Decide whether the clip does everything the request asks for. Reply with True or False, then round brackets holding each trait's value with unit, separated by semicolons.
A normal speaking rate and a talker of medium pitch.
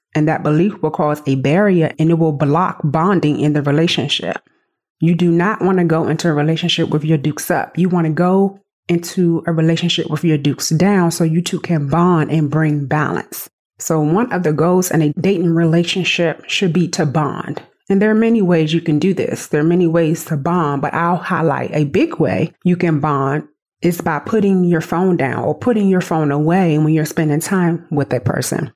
False (210 wpm; 165 Hz)